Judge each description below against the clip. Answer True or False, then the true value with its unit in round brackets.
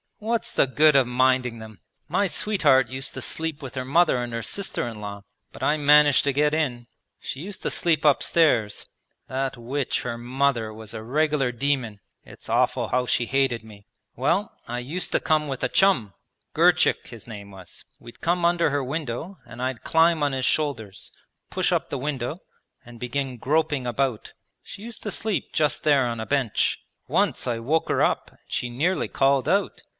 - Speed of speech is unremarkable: True (190 wpm)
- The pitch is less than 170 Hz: True (135 Hz)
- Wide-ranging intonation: False (4.4 semitones)